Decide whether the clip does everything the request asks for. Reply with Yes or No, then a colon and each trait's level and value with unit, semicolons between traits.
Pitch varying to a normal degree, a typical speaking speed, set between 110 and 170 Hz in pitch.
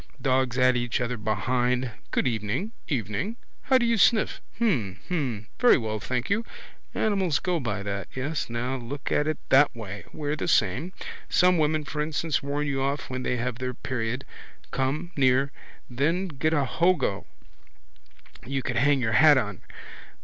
Yes: average, 4.3 semitones; average, 165 wpm; low, 135 Hz